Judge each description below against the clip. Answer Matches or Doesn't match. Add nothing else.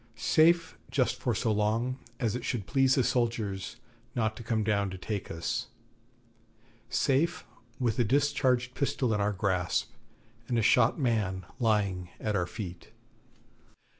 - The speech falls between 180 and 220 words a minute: Doesn't match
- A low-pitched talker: Matches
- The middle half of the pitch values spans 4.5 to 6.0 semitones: Doesn't match